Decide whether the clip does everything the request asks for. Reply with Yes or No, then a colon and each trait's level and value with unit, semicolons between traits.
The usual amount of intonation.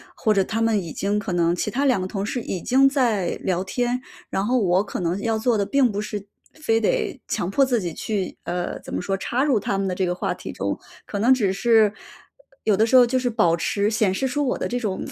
Yes: average, 4.3 semitones